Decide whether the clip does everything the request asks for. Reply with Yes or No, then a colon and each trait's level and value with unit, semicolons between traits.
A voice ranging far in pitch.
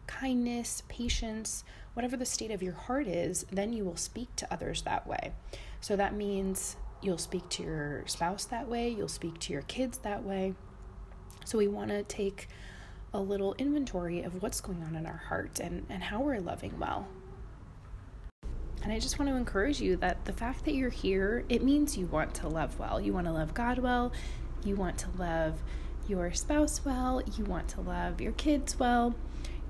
Yes: wide, 5.7 semitones